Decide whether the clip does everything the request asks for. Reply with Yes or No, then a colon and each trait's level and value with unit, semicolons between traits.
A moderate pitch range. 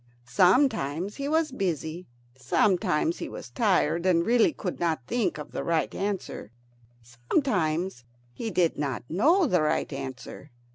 No: wide, 6.6 semitones